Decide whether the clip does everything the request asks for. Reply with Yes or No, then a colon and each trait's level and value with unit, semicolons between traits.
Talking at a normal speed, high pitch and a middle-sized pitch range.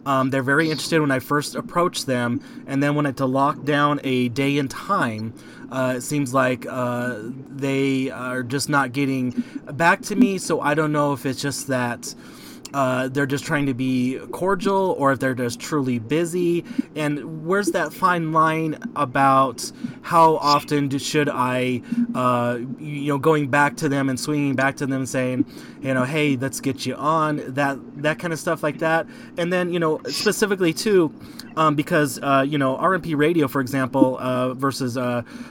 No: average, 190 wpm; medium, 140 Hz; average, 3.3 semitones